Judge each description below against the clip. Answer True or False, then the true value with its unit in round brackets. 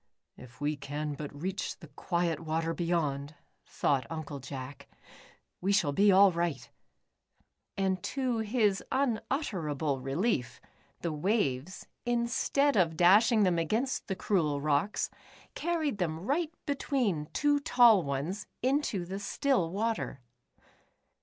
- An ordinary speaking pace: False (125 wpm)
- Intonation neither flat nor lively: False (7.2 semitones)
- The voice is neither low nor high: True (180 Hz)